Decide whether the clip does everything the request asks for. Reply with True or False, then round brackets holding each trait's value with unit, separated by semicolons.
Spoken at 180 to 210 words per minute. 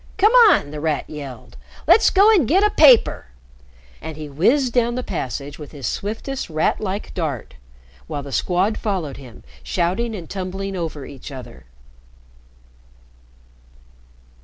False (140 wpm)